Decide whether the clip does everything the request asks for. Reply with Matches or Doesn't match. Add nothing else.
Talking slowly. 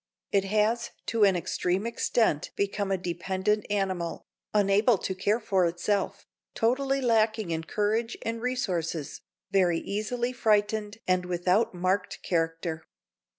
Matches